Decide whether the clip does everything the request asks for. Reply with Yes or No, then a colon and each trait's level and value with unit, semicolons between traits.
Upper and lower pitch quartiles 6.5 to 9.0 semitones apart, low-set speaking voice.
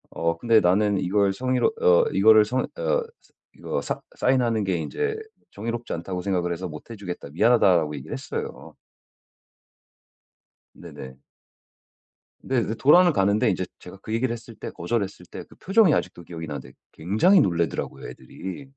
No: average, 5.2 semitones; low, 100 Hz